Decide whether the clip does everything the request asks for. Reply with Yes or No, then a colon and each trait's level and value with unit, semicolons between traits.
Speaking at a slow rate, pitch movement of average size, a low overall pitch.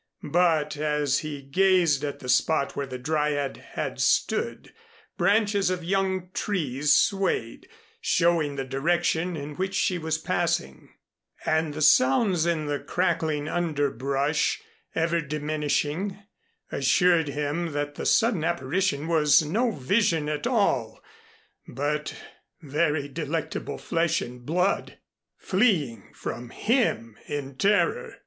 No: slow, 120 wpm; average, 3.8 semitones; medium, 155 Hz